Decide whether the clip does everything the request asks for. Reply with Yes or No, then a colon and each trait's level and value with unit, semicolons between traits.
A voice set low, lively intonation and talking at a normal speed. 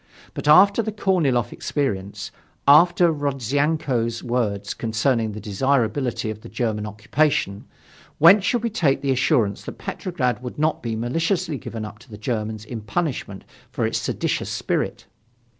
Yes: low, 125 Hz; wide, 6.0 semitones; average, 145 wpm